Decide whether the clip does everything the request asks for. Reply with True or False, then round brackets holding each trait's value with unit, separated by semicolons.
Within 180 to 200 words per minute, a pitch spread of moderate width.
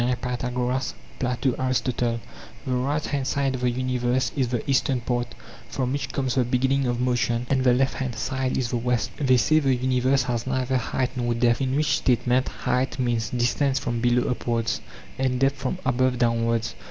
False (185 wpm; 1.4 semitones)